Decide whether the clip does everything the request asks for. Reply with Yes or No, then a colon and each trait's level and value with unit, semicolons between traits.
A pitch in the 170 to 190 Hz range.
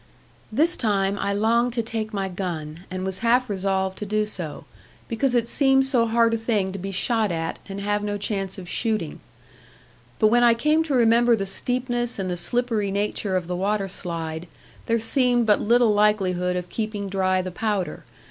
No: high, 210 Hz